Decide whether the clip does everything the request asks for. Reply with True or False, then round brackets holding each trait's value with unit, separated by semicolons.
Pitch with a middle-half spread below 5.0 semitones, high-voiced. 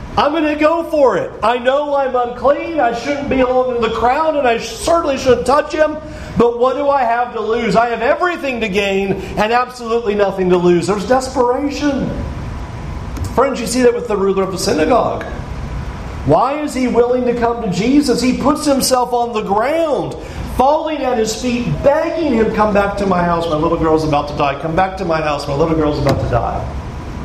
False (5.6 semitones; 240 Hz)